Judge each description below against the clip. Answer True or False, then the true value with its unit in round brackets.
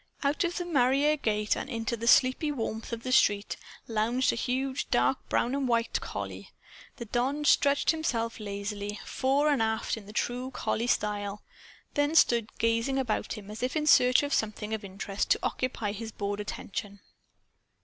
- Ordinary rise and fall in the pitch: True (4.2 semitones)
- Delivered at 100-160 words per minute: False (170 wpm)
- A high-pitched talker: True (235 Hz)